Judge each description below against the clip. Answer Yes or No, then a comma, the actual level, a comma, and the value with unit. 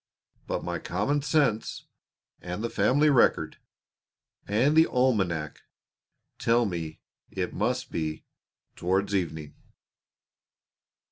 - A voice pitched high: No, low, 105 Hz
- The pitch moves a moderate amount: No, wide, 6.9 semitones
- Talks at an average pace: No, slow, 95 wpm